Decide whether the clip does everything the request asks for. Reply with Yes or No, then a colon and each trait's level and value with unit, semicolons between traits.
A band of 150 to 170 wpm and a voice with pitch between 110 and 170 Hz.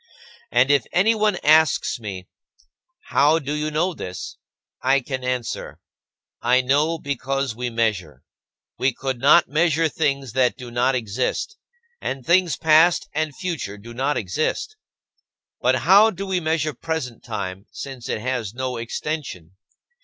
No: average, 140 wpm; low, 135 Hz